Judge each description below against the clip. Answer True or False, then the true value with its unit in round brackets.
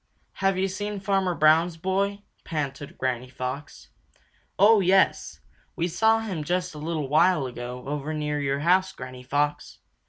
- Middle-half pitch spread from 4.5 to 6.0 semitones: True (5.1 semitones)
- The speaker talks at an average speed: True (150 wpm)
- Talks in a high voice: False (160 Hz)